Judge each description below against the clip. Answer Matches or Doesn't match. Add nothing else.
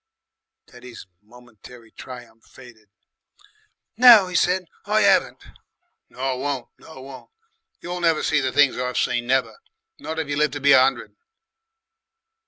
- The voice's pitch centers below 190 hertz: Matches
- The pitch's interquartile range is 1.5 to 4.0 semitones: Doesn't match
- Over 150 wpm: Doesn't match